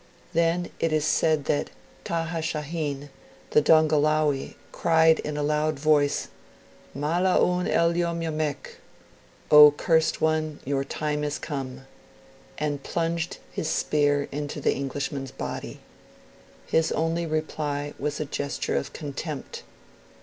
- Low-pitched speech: No, medium, 155 Hz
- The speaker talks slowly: Yes, slow, 125 wpm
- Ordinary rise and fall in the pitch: No, narrow, 1.9 semitones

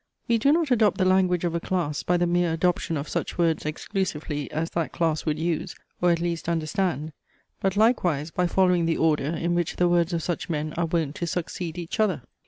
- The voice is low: No, medium, 170 Hz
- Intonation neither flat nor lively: No, narrow, 2.1 semitones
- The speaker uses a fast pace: Yes, fast, 215 wpm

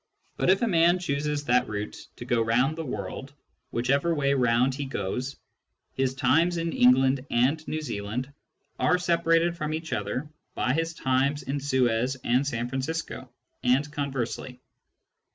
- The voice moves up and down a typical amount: Yes, average, 3.9 semitones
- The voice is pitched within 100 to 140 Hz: Yes, low, 135 Hz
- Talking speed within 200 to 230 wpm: No, average, 150 wpm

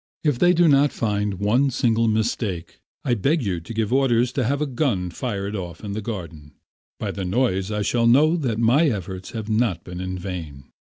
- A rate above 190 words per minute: Yes, fast, 205 wpm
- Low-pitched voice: Yes, low, 110 Hz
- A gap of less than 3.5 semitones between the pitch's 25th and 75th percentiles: No, average, 5.2 semitones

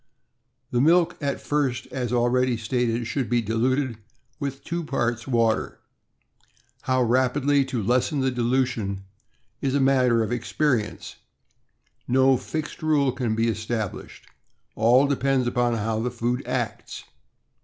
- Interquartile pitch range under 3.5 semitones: Yes, narrow, 2.6 semitones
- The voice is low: Yes, low, 125 Hz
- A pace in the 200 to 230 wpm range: No, slow, 135 wpm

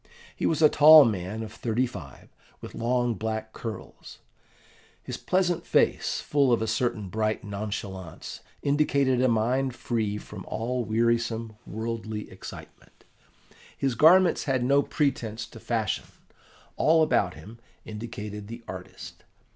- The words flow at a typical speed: No, slow, 130 wpm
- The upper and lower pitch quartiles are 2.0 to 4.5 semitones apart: Yes, average, 3.3 semitones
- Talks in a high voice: No, low, 115 Hz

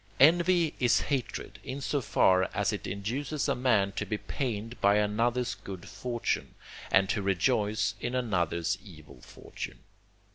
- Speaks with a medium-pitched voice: No, low, 110 Hz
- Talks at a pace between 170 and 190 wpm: No, average, 145 wpm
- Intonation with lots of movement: No, average, 4.5 semitones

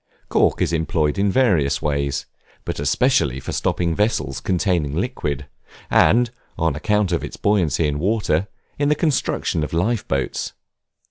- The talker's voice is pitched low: Yes, very low, 85 Hz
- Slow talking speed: No, average, 145 wpm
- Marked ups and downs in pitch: Yes, wide, 6.2 semitones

